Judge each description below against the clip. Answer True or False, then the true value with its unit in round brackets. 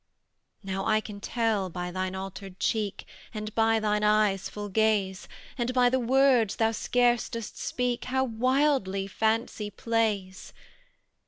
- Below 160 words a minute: True (140 wpm)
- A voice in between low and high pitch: False (215 Hz)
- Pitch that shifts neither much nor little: True (3.4 semitones)